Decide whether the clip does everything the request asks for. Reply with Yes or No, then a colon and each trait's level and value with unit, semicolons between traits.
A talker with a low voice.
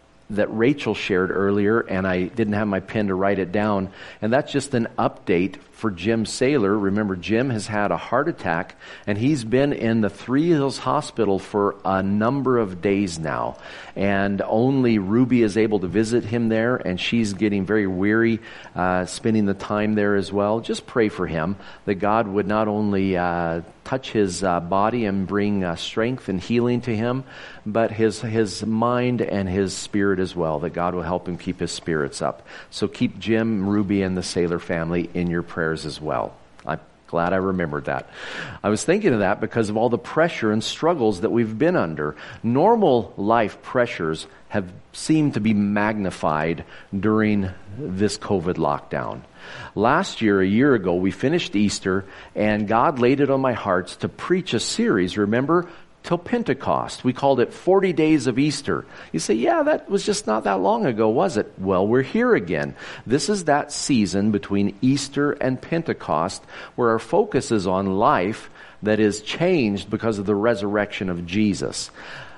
Yes: low, 105 Hz